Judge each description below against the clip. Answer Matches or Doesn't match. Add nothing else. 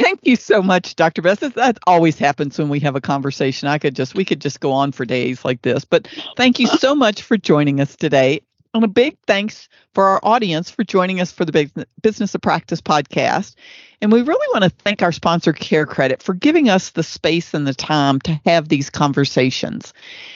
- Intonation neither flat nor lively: Doesn't match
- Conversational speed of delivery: Doesn't match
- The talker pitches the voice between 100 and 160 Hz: Doesn't match